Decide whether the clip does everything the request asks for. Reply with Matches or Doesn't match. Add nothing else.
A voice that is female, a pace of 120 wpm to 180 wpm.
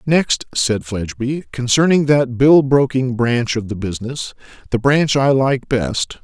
Doesn't match